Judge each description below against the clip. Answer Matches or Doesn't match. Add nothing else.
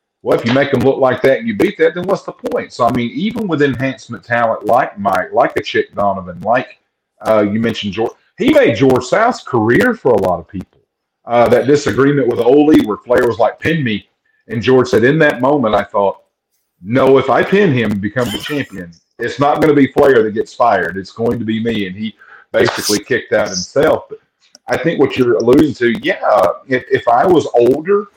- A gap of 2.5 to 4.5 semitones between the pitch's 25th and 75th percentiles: Doesn't match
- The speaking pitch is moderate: Doesn't match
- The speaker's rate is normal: Doesn't match